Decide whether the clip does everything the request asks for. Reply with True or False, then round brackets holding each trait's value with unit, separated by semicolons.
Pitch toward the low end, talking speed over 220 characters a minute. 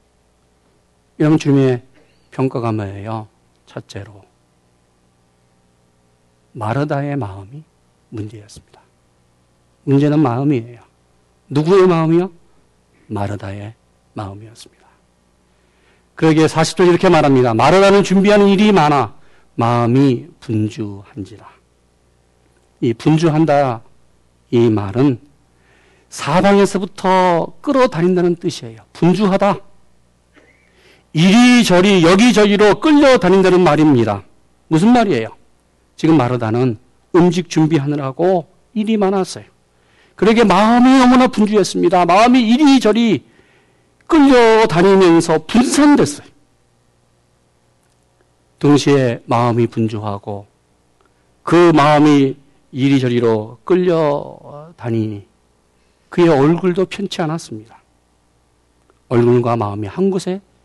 True (120 Hz; 235 characters per minute)